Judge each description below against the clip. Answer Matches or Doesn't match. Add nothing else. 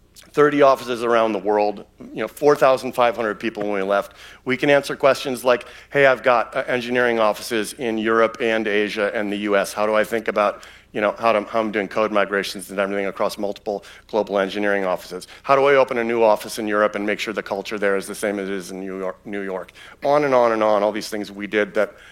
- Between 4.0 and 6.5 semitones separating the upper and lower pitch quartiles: Doesn't match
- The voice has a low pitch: Matches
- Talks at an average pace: Doesn't match